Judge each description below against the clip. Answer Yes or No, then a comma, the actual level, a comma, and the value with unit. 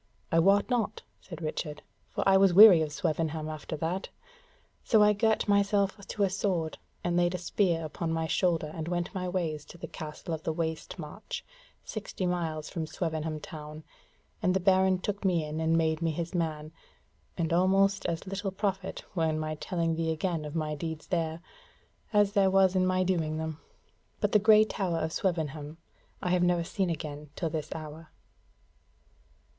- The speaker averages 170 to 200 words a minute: Yes, average, 185 wpm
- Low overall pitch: No, medium, 170 Hz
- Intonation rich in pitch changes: No, average, 3.2 semitones